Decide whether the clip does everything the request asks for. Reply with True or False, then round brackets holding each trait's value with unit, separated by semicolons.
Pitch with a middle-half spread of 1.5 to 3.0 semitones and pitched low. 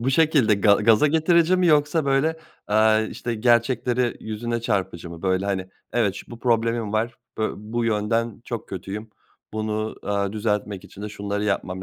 True (2.7 semitones; 110 Hz)